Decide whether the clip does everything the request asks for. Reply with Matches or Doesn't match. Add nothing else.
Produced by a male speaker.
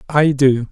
Matches